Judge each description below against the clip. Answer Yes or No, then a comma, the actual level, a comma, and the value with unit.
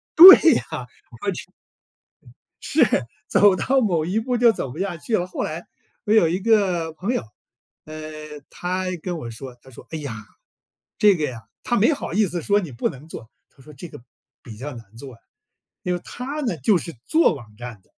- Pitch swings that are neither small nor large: No, wide, 6.9 semitones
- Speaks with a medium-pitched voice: Yes, medium, 170 Hz